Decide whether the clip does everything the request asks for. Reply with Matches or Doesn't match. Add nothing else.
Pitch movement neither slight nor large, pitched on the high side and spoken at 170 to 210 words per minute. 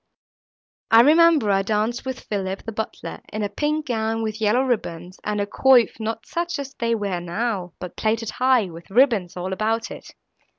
Matches